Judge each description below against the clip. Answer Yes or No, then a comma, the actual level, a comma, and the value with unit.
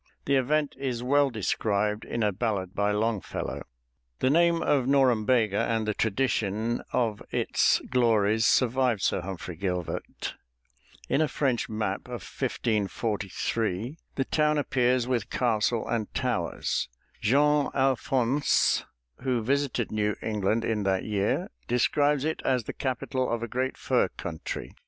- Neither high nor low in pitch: No, low, 115 Hz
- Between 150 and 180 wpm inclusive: No, slow, 135 wpm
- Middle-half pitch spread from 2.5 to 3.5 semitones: No, average, 3.9 semitones